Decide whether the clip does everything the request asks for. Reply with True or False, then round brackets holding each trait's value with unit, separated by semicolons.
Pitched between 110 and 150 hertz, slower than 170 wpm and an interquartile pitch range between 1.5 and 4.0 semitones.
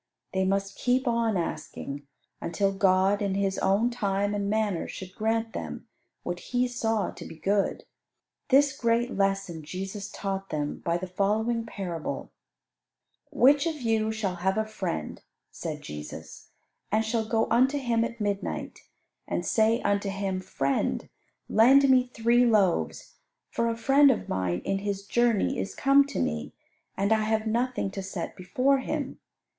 False (210 Hz; 155 wpm; 3.5 semitones)